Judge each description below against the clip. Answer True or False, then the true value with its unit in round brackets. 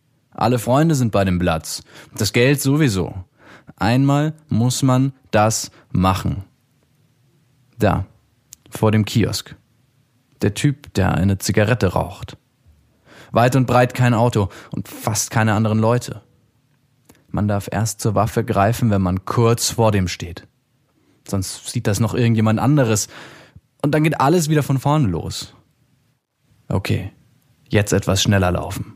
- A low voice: True (115 Hz)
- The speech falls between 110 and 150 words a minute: True (135 wpm)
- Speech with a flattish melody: False (4.7 semitones)